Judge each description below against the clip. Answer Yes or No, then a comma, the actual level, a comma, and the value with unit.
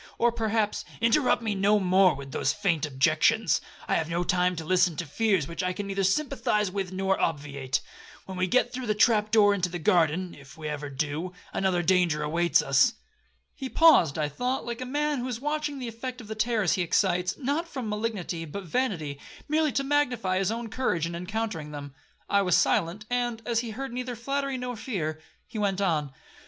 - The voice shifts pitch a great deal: Yes, wide, 5.9 semitones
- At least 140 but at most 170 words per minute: No, average, 200 wpm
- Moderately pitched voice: No, high, 200 Hz